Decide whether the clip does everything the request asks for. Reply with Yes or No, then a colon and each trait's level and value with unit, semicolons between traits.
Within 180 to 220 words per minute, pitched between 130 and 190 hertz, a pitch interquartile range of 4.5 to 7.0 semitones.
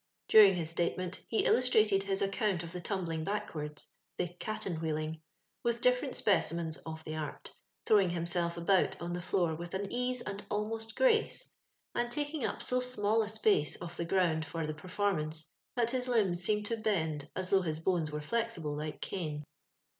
Yes: average, 195 wpm; medium, 185 Hz; average, 5.0 semitones